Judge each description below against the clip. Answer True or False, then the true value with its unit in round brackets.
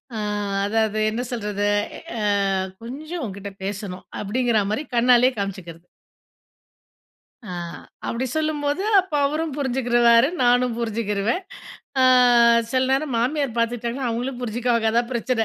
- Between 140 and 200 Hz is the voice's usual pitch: False (240 Hz)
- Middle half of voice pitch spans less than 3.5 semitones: True (3.1 semitones)